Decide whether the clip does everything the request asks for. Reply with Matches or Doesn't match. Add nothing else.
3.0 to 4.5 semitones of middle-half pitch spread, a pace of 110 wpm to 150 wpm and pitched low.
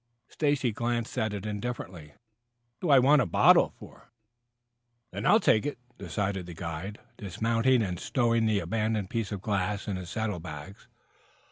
Doesn't match